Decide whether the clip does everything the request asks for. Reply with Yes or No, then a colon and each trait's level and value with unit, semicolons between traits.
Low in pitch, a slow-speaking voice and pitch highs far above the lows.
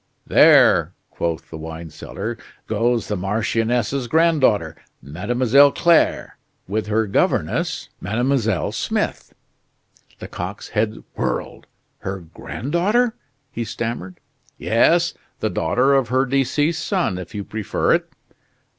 Yes: low, 115 Hz; slow, 110 wpm; wide, 5.7 semitones